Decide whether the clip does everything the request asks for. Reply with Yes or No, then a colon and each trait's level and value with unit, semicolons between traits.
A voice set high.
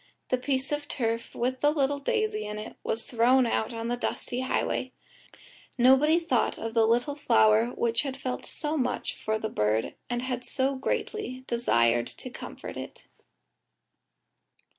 Yes: very high, 250 Hz